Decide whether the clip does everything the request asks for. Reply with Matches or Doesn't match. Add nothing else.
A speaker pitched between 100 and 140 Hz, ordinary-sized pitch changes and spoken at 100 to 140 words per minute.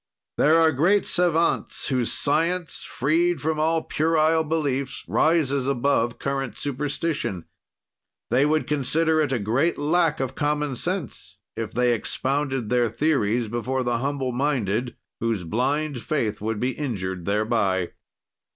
Matches